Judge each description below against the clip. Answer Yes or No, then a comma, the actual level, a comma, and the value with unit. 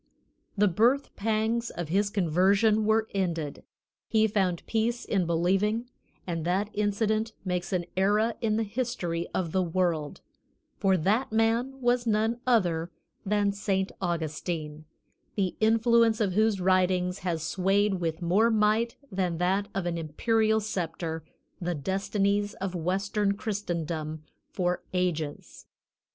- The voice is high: Yes, high, 195 Hz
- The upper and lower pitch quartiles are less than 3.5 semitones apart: No, average, 3.8 semitones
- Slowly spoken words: Yes, slow, 130 wpm